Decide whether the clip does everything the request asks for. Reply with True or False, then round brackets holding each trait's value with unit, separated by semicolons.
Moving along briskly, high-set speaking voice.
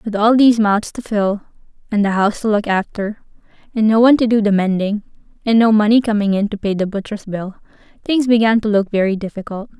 True (215 wpm; 210 Hz)